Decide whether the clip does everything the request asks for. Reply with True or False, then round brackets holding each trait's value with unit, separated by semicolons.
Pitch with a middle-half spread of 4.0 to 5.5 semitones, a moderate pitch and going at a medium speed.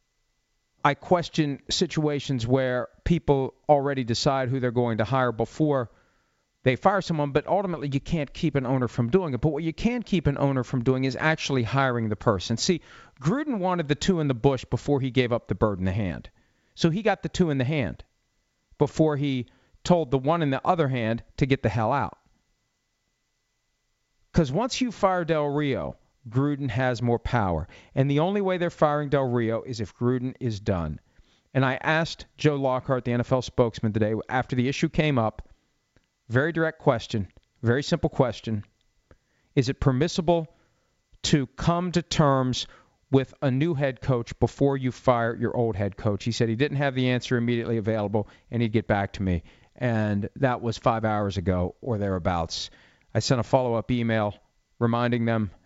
False (4.5 semitones; 130 Hz; 185 wpm)